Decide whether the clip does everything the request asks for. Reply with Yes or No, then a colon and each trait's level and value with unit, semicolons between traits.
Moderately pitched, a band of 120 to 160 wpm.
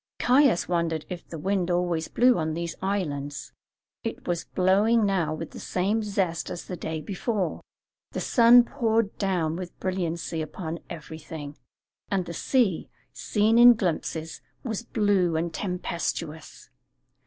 Yes: medium, 180 Hz; average, 140 wpm